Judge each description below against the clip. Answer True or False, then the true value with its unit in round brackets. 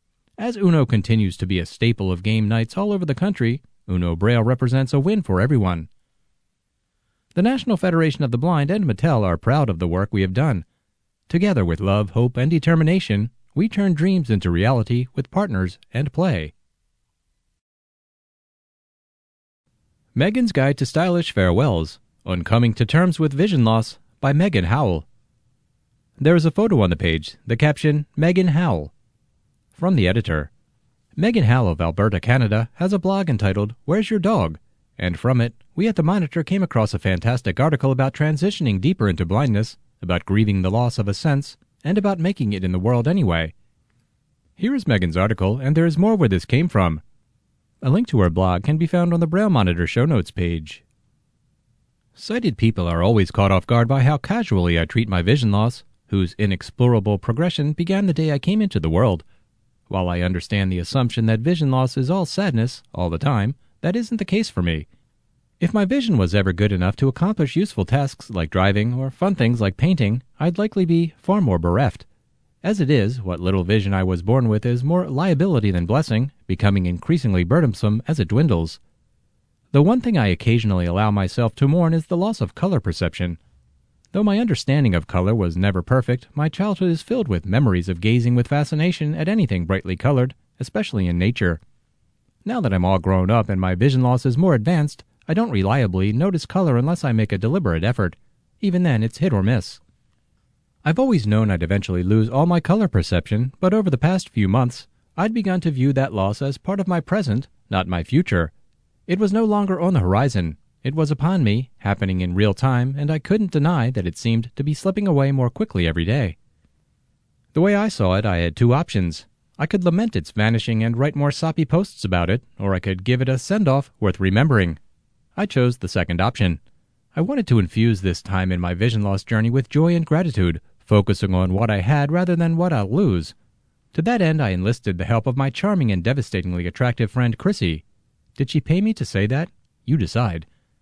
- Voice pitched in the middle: False (120 Hz)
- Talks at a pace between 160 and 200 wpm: True (195 wpm)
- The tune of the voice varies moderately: False (9.0 semitones)